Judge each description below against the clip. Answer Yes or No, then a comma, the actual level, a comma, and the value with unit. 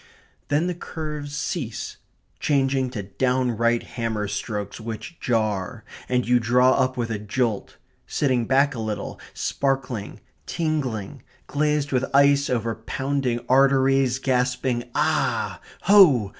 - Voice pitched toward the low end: Yes, low, 125 Hz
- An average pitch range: Yes, average, 3.3 semitones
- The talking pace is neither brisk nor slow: No, slow, 120 wpm